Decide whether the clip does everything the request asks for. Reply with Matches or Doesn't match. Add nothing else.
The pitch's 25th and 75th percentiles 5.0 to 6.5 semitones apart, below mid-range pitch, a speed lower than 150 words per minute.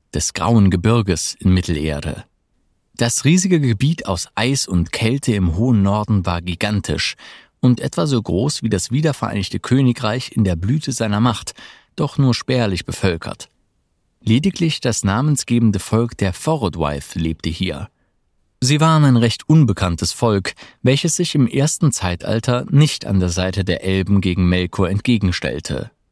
Matches